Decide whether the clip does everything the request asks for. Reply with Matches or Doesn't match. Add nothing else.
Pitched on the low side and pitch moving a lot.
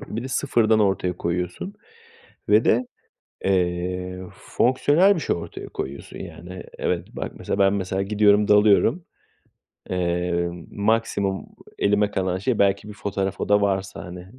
Doesn't match